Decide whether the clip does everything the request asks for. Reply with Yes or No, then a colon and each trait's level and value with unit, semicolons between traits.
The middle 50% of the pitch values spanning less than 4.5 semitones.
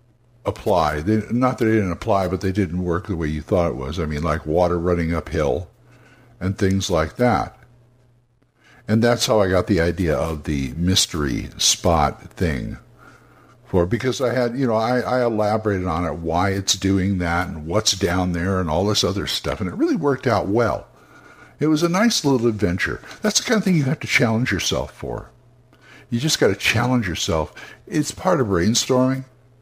No: wide, 5.6 semitones